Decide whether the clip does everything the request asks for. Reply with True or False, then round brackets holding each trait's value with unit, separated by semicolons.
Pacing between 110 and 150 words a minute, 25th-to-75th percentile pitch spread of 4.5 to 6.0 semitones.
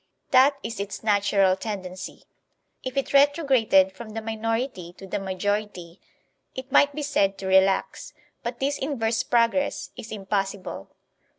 True (135 wpm; 5.0 semitones)